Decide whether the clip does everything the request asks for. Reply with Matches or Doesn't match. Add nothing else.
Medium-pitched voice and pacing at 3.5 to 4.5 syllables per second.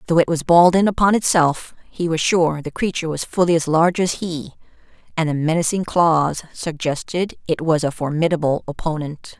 Doesn't match